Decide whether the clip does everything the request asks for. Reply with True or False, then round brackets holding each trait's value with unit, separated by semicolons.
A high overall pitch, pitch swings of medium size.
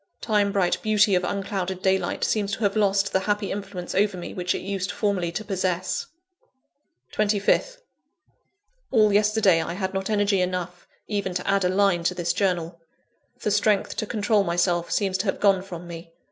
False (195 Hz; 2.2 semitones)